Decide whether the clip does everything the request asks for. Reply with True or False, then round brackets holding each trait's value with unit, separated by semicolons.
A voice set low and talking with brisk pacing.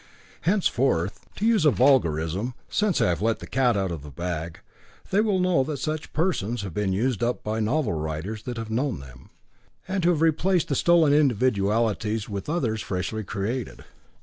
False (115 Hz; 180 wpm)